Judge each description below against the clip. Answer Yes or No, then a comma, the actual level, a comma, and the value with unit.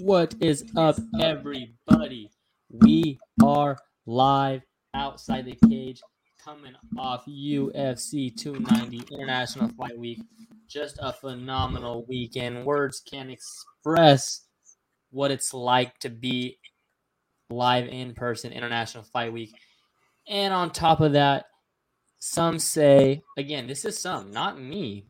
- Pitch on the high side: No, low, 135 Hz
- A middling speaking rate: No, slow, 115 wpm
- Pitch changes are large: No, average, 4.1 semitones